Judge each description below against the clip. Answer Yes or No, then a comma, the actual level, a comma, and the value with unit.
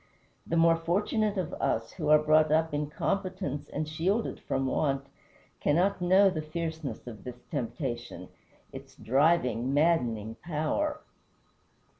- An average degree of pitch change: Yes, average, 4.3 semitones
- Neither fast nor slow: No, slow, 130 wpm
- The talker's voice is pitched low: No, medium, 155 Hz